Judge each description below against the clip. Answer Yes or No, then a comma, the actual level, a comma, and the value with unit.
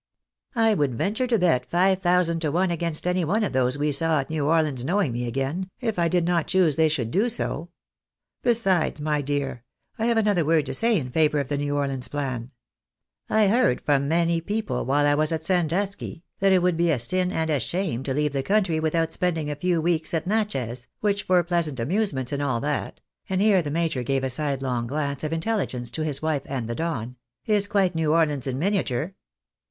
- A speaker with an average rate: No, fast, 220 wpm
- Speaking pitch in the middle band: Yes, medium, 160 Hz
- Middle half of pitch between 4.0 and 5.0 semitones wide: Yes, average, 4.7 semitones